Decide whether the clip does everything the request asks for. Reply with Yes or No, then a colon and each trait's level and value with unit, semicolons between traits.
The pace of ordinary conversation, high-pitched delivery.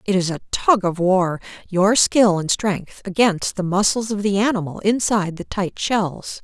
Yes: average, 185 wpm; high, 195 Hz